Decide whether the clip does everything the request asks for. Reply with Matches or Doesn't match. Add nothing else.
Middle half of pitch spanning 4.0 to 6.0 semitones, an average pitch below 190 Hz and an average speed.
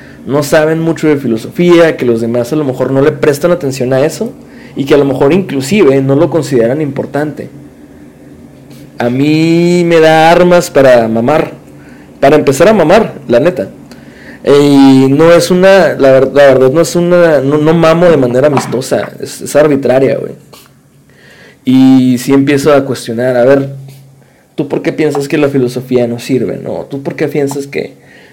Doesn't match